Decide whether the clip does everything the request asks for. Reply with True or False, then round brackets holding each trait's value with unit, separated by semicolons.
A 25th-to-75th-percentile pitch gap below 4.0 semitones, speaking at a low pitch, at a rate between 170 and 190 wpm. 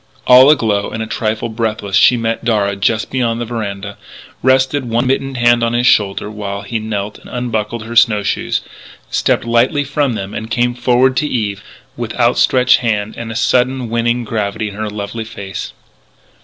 True (2.6 semitones; 115 Hz; 185 wpm)